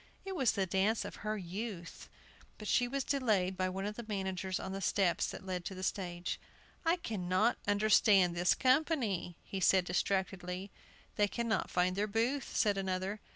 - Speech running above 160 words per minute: Yes, average, 175 wpm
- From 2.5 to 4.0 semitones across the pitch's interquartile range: Yes, average, 3.2 semitones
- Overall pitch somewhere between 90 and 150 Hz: No, high, 195 Hz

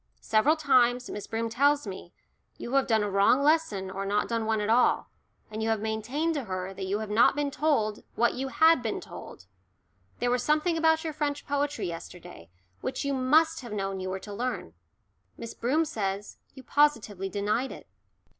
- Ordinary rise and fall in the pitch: No, wide, 5.8 semitones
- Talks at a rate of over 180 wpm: Yes, average, 190 wpm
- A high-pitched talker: Yes, high, 235 Hz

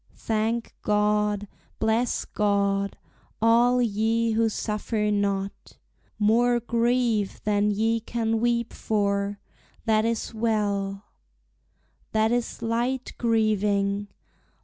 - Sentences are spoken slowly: Yes, slow, 95 wpm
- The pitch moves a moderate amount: No, narrow, 2.0 semitones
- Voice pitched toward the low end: No, high, 220 Hz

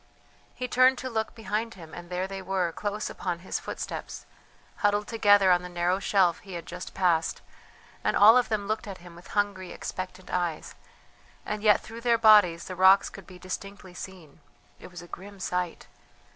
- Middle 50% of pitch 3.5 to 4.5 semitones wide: No, average, 2.8 semitones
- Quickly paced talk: No, average, 185 wpm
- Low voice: No, high, 190 Hz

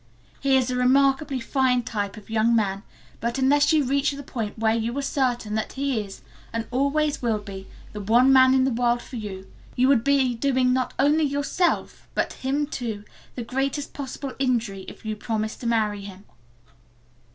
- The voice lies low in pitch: No, very high, 250 Hz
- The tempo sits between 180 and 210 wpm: Yes, average, 185 wpm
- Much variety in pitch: No, average, 3.7 semitones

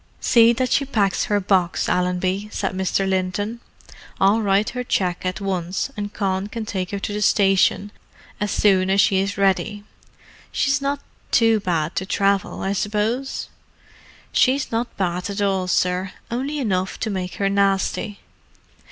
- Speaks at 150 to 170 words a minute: Yes, average, 160 wpm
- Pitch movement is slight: Yes, narrow, 2.3 semitones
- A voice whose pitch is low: No, high, 200 Hz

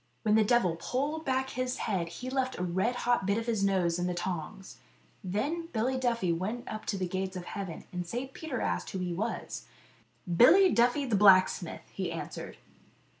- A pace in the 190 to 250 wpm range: Yes, average, 200 wpm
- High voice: Yes, high, 210 Hz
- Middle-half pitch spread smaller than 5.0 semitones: No, wide, 5.6 semitones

